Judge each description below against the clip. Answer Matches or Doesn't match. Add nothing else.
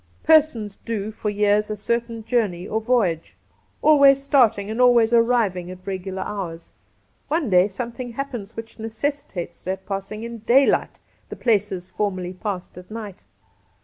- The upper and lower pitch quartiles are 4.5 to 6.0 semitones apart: Doesn't match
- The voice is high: Matches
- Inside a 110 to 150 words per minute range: Matches